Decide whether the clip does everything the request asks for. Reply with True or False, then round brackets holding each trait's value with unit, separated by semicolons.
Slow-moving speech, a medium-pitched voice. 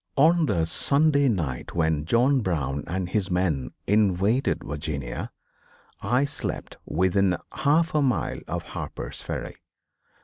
False (125 wpm; 95 Hz)